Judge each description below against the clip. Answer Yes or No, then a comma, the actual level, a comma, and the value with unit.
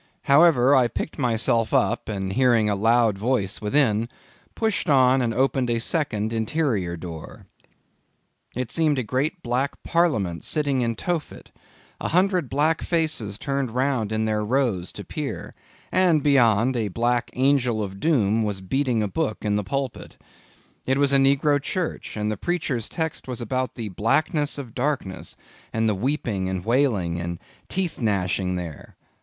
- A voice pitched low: Yes, low, 120 Hz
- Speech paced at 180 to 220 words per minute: No, average, 160 wpm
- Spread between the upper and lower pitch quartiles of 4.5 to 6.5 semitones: Yes, average, 5.1 semitones